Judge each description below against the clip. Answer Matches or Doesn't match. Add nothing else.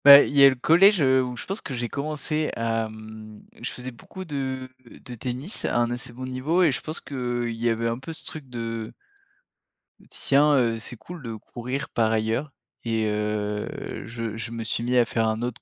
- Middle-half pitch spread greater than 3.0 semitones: Matches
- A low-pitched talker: Matches